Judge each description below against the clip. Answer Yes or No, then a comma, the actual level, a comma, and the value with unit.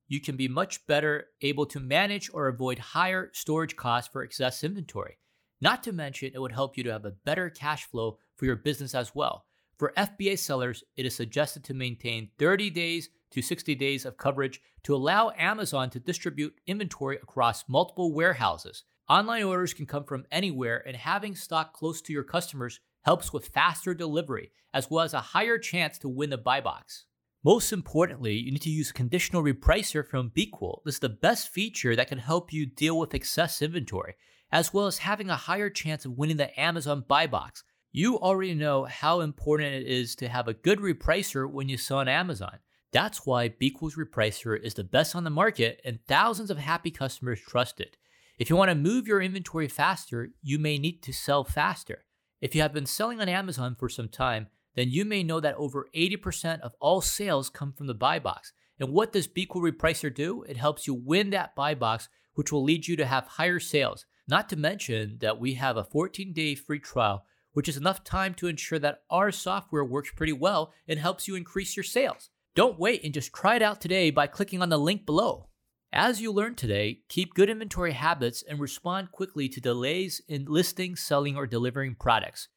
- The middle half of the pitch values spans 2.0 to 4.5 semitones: No, average, 5.1 semitones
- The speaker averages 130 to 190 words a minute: No, average, 200 wpm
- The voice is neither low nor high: Yes, medium, 150 Hz